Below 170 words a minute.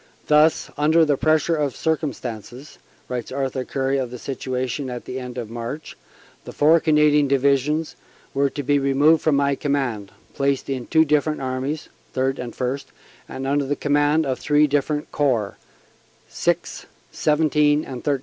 Yes: average, 160 wpm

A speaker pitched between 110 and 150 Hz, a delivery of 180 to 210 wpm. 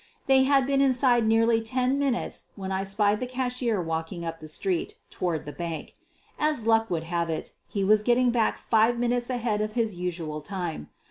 No: high, 220 Hz; average, 190 wpm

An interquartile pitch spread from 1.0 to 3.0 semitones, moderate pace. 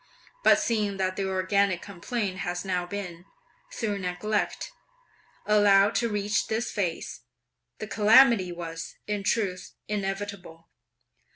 No: narrow, 2.5 semitones; slow, 115 wpm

